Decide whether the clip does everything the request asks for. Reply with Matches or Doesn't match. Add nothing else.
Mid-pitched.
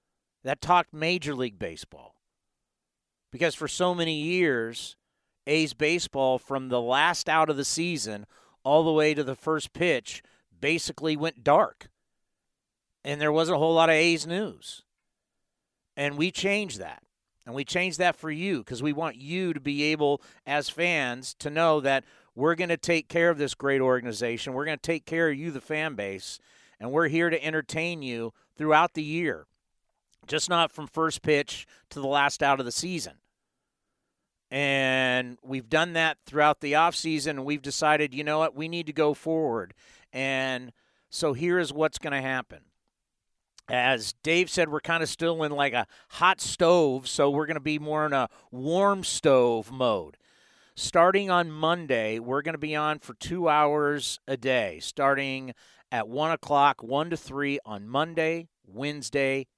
Matches